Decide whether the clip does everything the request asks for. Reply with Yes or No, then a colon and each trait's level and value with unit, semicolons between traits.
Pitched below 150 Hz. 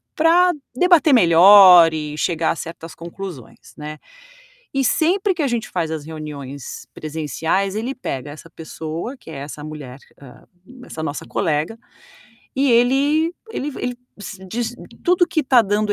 No: medium, 185 Hz